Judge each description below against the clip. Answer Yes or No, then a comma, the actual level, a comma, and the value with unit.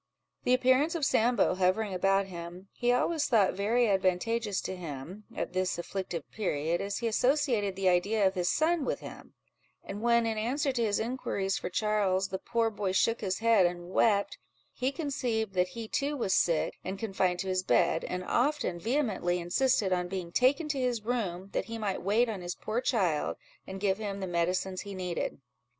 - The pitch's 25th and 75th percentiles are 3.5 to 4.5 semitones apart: Yes, average, 4.2 semitones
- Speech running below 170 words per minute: No, average, 190 wpm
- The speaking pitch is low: No, high, 200 Hz